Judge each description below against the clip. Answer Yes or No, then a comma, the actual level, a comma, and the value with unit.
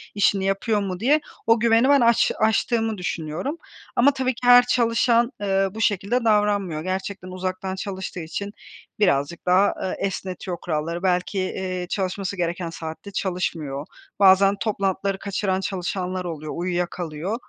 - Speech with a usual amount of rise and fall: Yes, average, 3.0 semitones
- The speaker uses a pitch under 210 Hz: Yes, high, 190 Hz